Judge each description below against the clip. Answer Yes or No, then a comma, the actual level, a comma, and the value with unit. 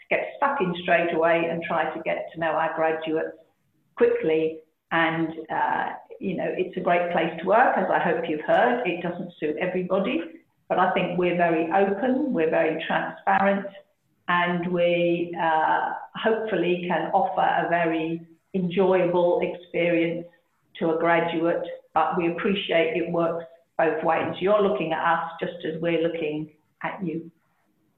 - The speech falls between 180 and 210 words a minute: No, average, 155 wpm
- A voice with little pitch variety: Yes, narrow, 2.2 semitones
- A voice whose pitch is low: No, medium, 170 Hz